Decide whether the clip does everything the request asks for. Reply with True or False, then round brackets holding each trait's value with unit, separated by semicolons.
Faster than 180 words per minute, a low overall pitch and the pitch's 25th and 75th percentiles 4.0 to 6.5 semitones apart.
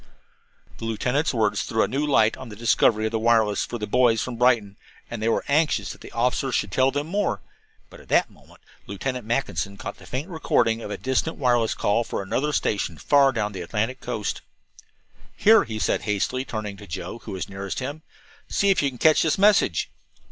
True (205 wpm; 115 Hz; 4.4 semitones)